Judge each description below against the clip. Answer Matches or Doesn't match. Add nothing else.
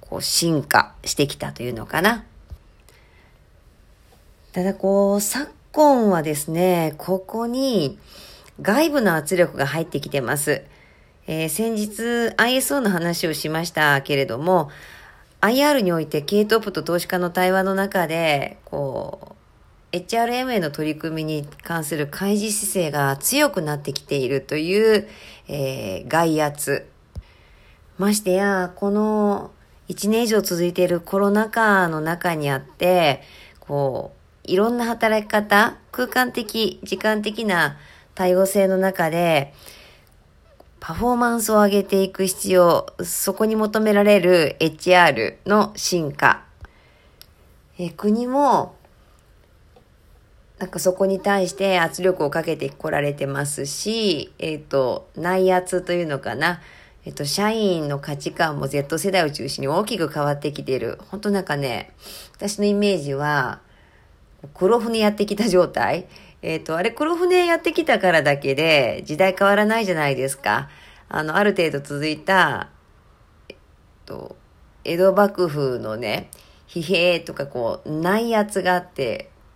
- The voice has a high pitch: Doesn't match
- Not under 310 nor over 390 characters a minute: Doesn't match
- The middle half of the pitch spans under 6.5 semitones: Matches